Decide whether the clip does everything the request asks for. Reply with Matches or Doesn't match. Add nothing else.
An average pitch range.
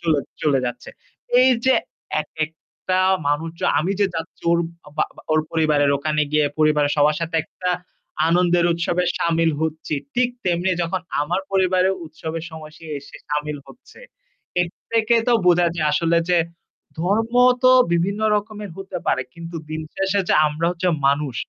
Matches